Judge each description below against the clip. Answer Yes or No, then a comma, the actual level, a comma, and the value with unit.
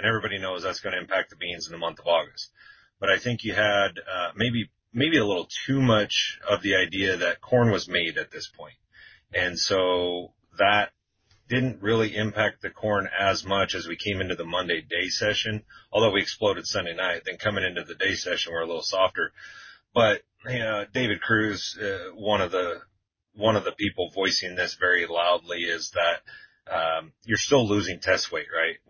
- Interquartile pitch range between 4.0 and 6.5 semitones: No, average, 3.5 semitones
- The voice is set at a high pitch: No, low, 105 Hz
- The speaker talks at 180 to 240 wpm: Yes, average, 195 wpm